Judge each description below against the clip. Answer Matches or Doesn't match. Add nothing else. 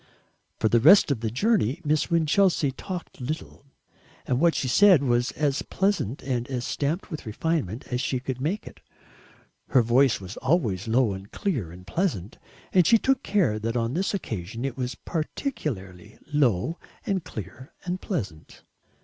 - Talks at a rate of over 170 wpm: Doesn't match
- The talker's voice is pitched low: Matches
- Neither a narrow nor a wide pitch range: Doesn't match